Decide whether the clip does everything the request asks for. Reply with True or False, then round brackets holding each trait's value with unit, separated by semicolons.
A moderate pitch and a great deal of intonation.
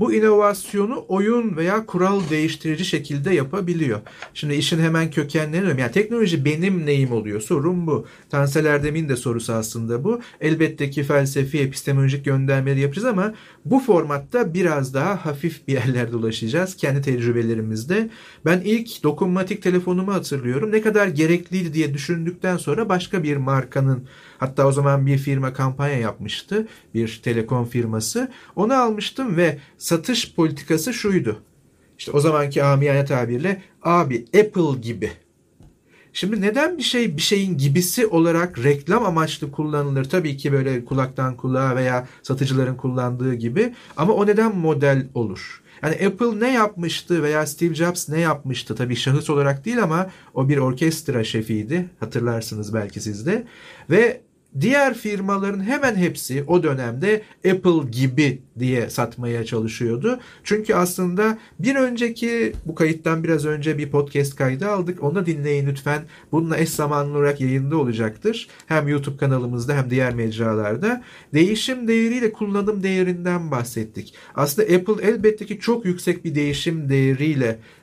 True (155 Hz; 6.1 semitones)